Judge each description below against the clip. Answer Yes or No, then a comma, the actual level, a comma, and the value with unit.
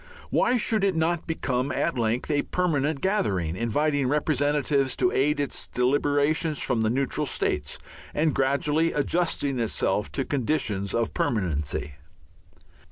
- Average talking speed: No, slow, 130 wpm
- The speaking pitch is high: No, medium, 140 Hz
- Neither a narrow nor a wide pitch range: Yes, average, 4.9 semitones